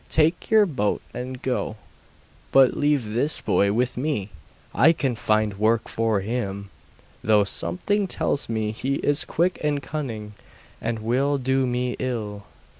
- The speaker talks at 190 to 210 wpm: No, average, 145 wpm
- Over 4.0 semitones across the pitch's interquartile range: Yes, average, 5.0 semitones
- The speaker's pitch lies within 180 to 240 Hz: No, low, 125 Hz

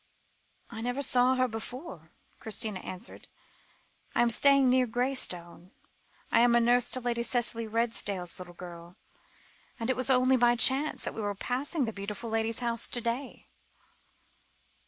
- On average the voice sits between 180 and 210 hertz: No, high, 235 Hz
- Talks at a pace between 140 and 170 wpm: Yes, average, 150 wpm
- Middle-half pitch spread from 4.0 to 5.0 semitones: No, average, 2.9 semitones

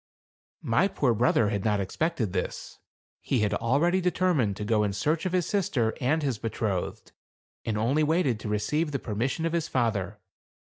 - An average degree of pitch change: No, wide, 7.2 semitones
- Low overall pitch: Yes, low, 120 Hz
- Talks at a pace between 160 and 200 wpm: Yes, average, 180 wpm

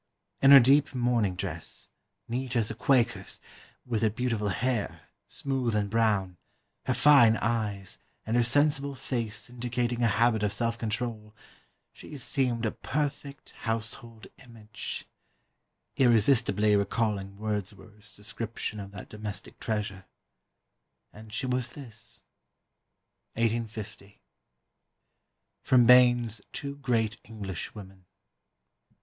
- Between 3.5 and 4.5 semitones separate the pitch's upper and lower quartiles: No, average, 2.8 semitones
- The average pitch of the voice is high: No, low, 115 Hz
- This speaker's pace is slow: Yes, slow, 110 wpm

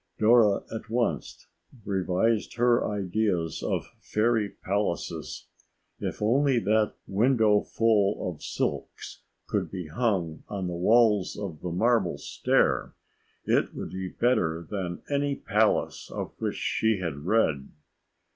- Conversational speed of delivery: No, slow, 120 wpm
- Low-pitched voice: Yes, low, 105 Hz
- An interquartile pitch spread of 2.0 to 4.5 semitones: Yes, average, 4.0 semitones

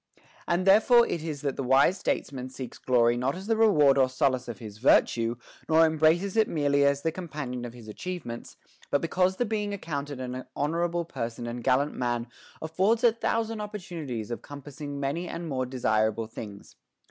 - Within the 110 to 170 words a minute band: No, average, 185 wpm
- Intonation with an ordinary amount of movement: No, wide, 5.7 semitones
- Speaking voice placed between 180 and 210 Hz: No, medium, 145 Hz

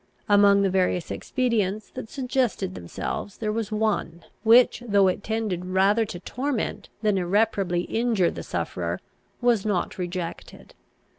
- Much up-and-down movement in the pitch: No, average, 3.5 semitones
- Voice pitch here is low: No, high, 205 Hz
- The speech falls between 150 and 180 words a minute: No, slow, 135 wpm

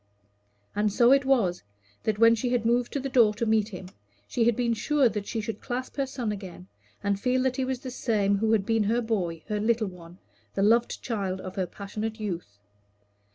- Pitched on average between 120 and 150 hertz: No, high, 220 Hz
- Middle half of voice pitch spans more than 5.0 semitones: No, average, 3.3 semitones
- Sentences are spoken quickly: Yes, fast, 215 wpm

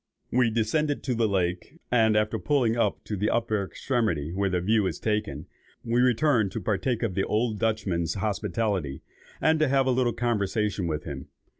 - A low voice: Yes, low, 110 Hz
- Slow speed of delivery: No, average, 175 wpm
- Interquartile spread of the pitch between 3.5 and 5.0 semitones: Yes, average, 3.8 semitones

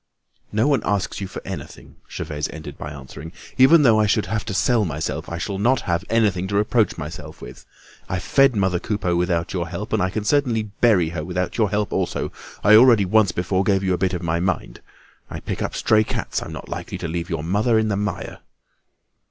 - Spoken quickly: Yes, fast, 215 wpm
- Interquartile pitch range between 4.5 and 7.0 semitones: No, average, 4.0 semitones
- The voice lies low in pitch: Yes, very low, 95 Hz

